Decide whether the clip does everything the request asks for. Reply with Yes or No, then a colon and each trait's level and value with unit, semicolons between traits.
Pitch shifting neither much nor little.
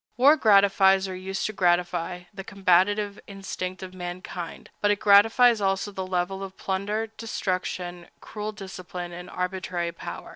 No: narrow, 2.1 semitones